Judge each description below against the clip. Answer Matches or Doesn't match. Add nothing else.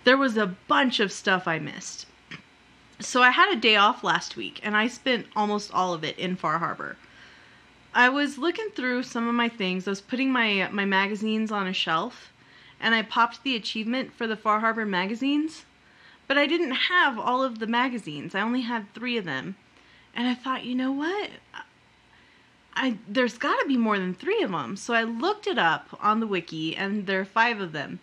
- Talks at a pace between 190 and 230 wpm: Matches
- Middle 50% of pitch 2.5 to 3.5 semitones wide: Doesn't match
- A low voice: Doesn't match